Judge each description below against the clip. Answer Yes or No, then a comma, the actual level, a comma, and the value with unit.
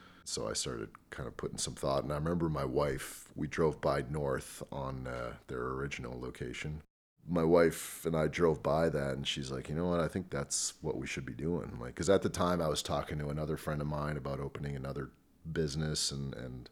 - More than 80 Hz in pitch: No, very low, 75 Hz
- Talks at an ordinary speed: No, fast, 225 wpm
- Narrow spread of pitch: Yes, narrow, 2.3 semitones